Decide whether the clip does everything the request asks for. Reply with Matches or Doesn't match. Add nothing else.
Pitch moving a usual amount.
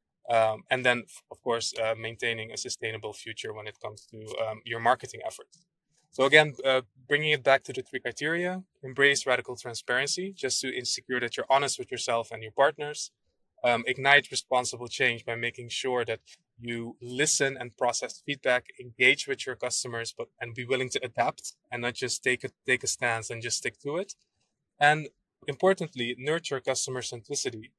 Matches